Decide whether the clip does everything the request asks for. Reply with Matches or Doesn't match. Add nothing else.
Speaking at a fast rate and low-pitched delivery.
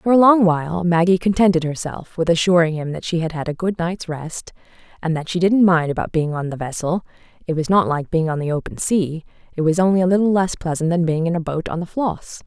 Doesn't match